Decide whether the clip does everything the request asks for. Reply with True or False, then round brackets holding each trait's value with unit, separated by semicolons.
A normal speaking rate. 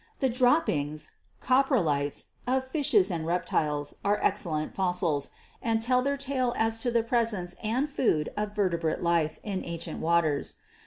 True (150 wpm)